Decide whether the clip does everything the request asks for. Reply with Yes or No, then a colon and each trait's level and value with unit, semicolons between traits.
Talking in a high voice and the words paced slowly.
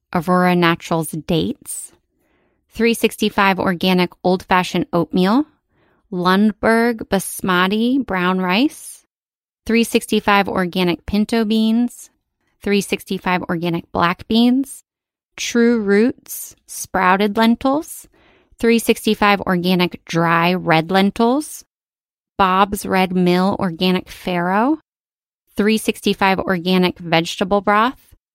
Yes: high, 195 Hz; slow, 80 wpm